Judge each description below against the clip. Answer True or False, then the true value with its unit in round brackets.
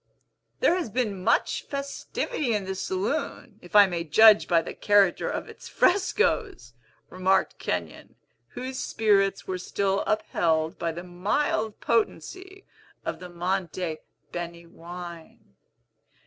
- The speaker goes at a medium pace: False (125 wpm)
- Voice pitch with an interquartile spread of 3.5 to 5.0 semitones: True (4.7 semitones)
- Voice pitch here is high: True (195 Hz)